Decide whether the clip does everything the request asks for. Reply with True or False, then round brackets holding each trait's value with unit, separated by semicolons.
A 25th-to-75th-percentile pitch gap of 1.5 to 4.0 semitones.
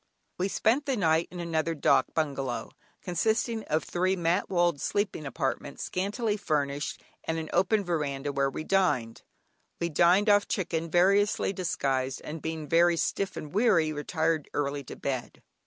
False (4.6 semitones)